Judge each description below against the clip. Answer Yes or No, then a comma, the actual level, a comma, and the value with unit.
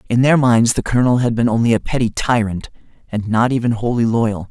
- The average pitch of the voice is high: No, low, 115 Hz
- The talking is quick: Yes, fast, 215 wpm